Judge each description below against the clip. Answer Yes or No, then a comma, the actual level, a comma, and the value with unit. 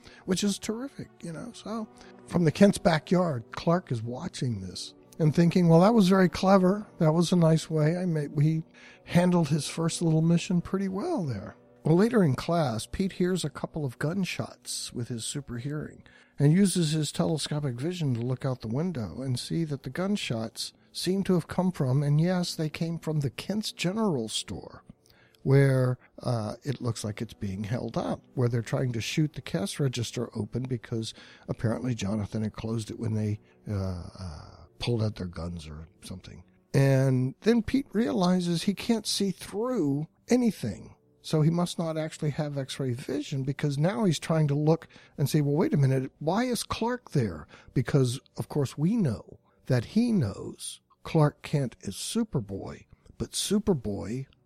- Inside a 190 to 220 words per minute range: No, average, 180 wpm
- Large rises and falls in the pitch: Yes, wide, 6.6 semitones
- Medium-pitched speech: Yes, medium, 145 Hz